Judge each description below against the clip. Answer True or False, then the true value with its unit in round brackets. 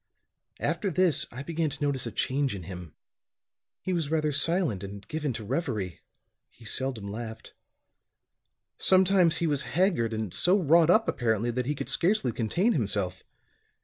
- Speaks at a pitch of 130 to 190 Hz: True (140 Hz)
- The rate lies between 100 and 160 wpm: True (155 wpm)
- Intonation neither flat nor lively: False (7.1 semitones)